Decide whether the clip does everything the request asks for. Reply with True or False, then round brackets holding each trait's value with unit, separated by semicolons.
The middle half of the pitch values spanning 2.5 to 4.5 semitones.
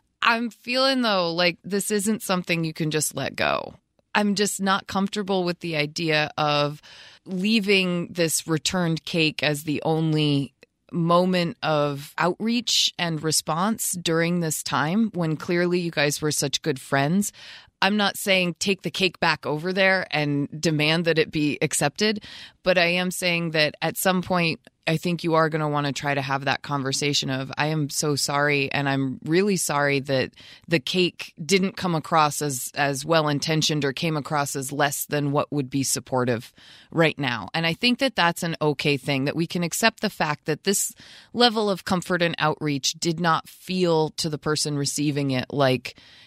True (3.8 semitones)